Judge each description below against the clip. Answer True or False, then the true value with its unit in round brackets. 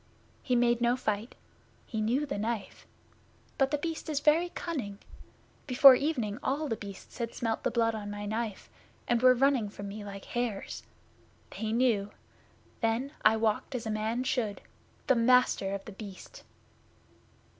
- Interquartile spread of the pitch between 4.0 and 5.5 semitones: False (3.3 semitones)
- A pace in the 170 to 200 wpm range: False (160 wpm)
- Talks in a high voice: True (230 Hz)